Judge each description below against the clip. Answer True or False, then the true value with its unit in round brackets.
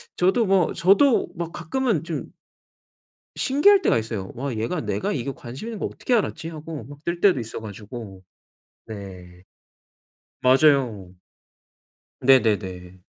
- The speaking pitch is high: False (140 Hz)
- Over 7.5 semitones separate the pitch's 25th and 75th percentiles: True (8.6 semitones)